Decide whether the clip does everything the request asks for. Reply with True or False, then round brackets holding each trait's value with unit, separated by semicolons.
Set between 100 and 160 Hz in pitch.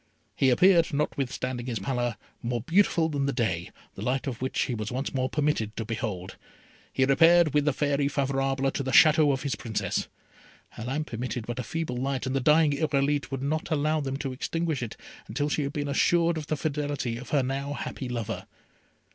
True (135 Hz)